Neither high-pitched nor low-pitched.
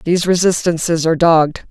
Yes: medium, 170 Hz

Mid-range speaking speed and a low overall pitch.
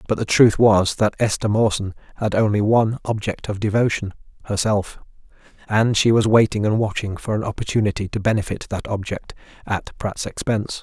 Yes: average, 150 wpm; low, 105 Hz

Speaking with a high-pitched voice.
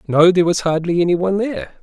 No: medium, 180 Hz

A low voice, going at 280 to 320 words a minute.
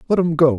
No: medium, 155 Hz; fast, 310 wpm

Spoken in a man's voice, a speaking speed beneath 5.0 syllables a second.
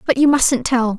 No: female; 4.6 syllables/s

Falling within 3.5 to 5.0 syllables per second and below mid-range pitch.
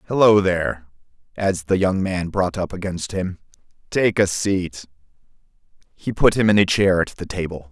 Yes: 4.8 syllables/s; very low, 95 Hz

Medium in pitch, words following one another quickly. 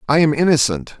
No: medium, 145 Hz; average, 180 wpm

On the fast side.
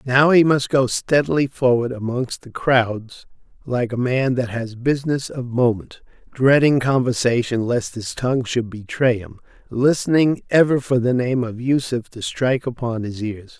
No: average, 165 wpm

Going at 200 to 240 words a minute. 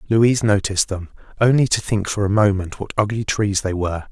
Yes: fast, 205 wpm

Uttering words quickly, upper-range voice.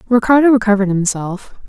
No: slow, 105 wpm; high, 215 Hz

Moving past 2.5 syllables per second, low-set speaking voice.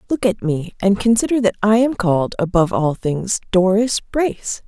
No: 5.0 syllables/s; high, 205 Hz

